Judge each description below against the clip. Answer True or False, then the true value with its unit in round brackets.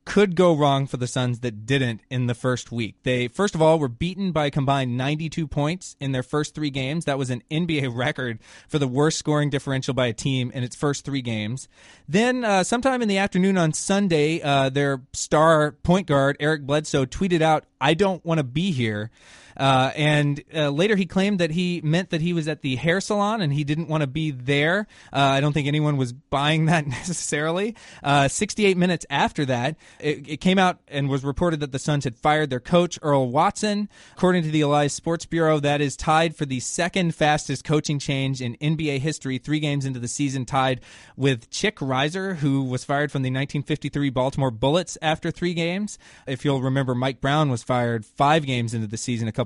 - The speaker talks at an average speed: False (210 wpm)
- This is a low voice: False (150 Hz)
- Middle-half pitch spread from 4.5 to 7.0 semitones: False (3.6 semitones)